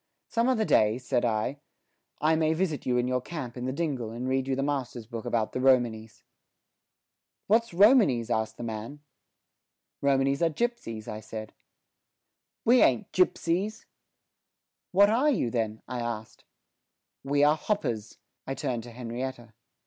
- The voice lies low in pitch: Yes, low, 130 Hz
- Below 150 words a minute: No, average, 155 wpm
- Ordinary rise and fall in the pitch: No, wide, 5.8 semitones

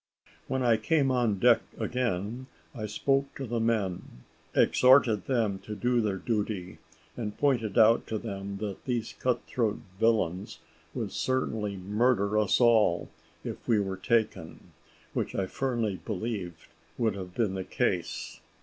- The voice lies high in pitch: No, low, 110 Hz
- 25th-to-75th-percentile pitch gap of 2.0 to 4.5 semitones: Yes, average, 3.6 semitones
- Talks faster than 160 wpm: No, average, 145 wpm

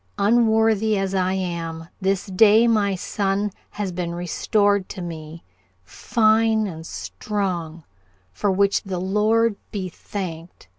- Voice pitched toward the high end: Yes, high, 195 Hz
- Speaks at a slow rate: Yes, slow, 120 wpm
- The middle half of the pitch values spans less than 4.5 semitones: Yes, average, 3.3 semitones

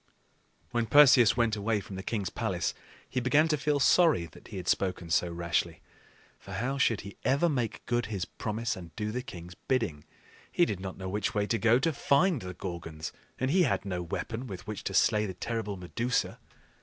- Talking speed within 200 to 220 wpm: Yes, fast, 205 wpm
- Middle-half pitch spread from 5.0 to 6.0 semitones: Yes, average, 5.3 semitones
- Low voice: Yes, low, 110 Hz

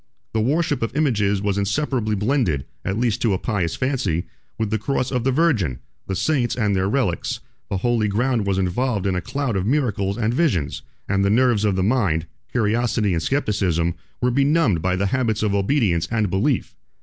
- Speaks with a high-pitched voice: No, low, 110 Hz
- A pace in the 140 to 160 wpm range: No, average, 185 wpm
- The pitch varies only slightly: No, average, 4.8 semitones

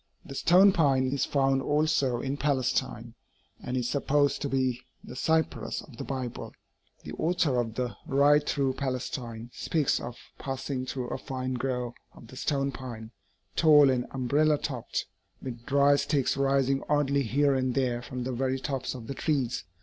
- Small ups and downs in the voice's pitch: Yes, narrow, 2.1 semitones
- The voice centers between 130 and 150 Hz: Yes, low, 135 Hz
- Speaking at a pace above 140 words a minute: Yes, average, 165 wpm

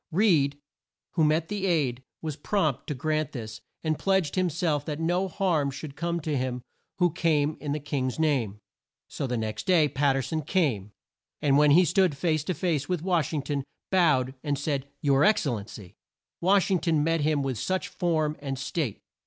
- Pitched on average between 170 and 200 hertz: No, medium, 150 Hz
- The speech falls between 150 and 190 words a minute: No, average, 200 wpm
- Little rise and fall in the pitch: No, average, 3.8 semitones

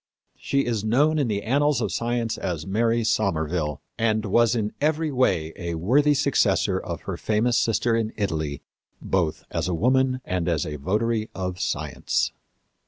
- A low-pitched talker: Yes, low, 110 Hz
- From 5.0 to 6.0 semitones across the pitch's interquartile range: Yes, average, 5.3 semitones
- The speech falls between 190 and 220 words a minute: No, average, 165 wpm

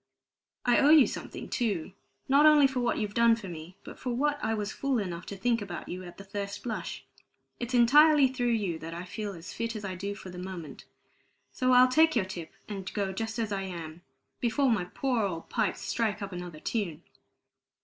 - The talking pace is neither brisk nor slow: No, fast, 210 wpm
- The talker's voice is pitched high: Yes, high, 210 Hz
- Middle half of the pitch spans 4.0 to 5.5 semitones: Yes, average, 4.9 semitones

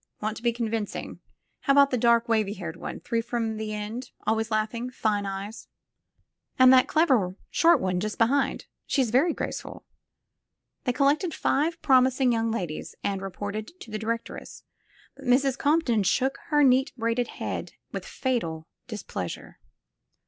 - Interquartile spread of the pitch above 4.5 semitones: No, average, 3.5 semitones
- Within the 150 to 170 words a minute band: Yes, average, 160 wpm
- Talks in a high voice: Yes, high, 230 Hz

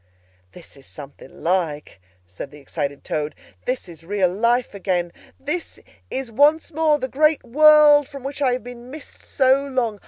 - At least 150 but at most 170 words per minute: Yes, average, 165 wpm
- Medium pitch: No, high, 245 Hz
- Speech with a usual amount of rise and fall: No, wide, 8.5 semitones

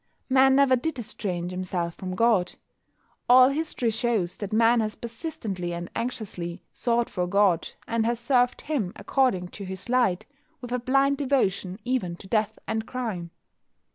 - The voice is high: Yes, high, 225 Hz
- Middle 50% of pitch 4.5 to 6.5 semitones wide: Yes, wide, 5.5 semitones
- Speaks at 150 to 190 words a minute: Yes, average, 155 wpm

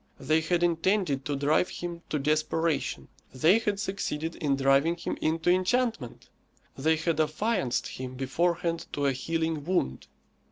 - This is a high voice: No, medium, 160 Hz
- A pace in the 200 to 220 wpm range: No, average, 145 wpm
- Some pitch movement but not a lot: Yes, average, 3.6 semitones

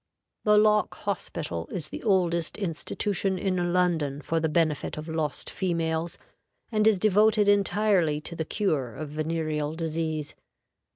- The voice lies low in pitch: No, medium, 170 Hz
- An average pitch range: Yes, average, 4.3 semitones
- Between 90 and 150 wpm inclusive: Yes, slow, 135 wpm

